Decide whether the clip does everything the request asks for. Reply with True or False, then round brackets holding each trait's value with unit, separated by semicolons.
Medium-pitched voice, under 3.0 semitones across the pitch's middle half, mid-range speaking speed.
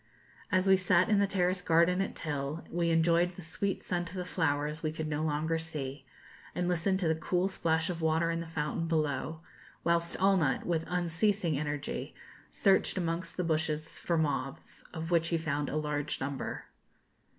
True (165 Hz; 2.5 semitones; 185 wpm)